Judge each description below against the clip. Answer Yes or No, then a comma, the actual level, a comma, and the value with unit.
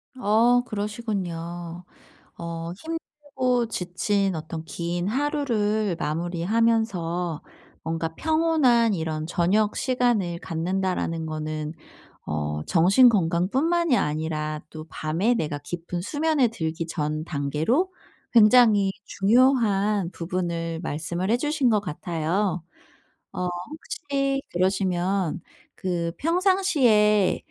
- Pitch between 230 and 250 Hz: No, high, 190 Hz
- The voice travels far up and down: Yes, wide, 6.4 semitones